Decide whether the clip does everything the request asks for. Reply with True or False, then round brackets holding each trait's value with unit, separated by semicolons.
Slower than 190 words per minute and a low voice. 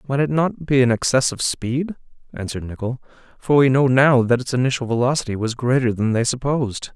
False (200 wpm; 125 Hz)